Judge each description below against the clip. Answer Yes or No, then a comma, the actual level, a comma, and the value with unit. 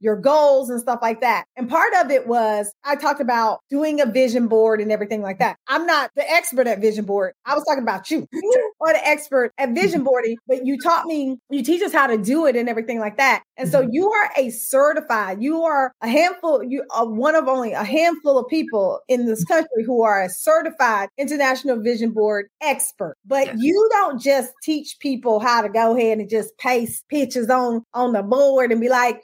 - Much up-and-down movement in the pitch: No, average, 4.2 semitones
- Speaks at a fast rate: Yes, fast, 220 wpm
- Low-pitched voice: No, very high, 260 Hz